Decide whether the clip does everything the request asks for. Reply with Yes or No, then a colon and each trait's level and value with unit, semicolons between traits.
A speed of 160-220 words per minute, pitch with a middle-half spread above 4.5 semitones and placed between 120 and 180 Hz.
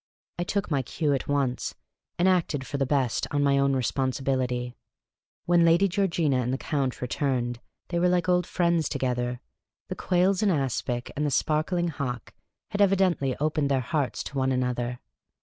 Yes: average, 180 wpm; average, 5.0 semitones; medium, 140 Hz